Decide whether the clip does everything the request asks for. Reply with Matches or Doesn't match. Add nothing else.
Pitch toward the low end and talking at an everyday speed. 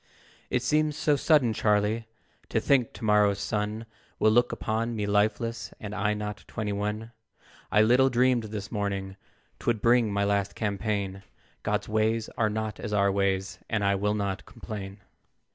Matches